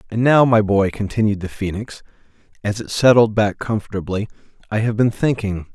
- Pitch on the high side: No, low, 105 Hz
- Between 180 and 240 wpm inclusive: No, average, 165 wpm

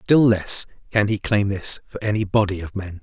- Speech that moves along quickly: Yes, fast, 220 wpm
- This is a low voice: Yes, low, 100 Hz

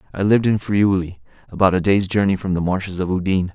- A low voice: Yes, very low, 95 Hz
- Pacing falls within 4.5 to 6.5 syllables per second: No, 6.7 syllables/s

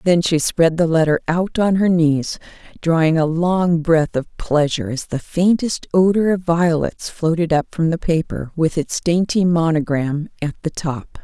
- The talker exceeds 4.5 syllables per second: No, 4.4 syllables/s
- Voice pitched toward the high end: No, medium, 165 Hz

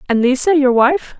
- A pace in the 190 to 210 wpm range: Yes, average, 200 wpm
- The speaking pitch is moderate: No, very high, 270 Hz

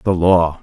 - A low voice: Yes, very low, 85 Hz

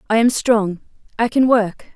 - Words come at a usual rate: Yes, average, 185 wpm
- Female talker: Yes, female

